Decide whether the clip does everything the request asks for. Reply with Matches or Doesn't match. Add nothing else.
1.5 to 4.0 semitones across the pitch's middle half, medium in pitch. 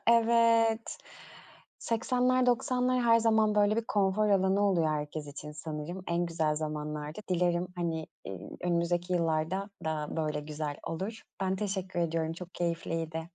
Doesn't match